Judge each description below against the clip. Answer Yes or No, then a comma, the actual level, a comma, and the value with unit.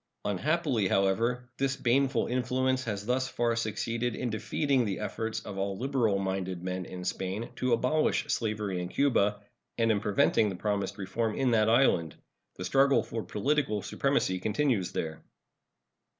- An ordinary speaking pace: Yes, average, 150 wpm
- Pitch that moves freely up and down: No, average, 4.5 semitones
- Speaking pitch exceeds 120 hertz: No, low, 110 Hz